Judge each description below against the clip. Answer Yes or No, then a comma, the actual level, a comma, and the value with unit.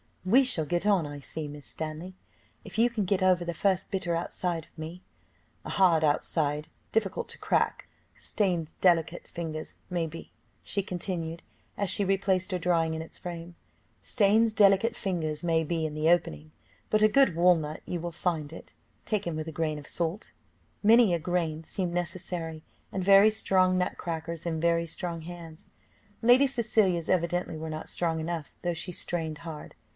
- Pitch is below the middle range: No, medium, 175 Hz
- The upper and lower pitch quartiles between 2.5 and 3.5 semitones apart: Yes, average, 2.8 semitones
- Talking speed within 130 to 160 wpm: No, average, 175 wpm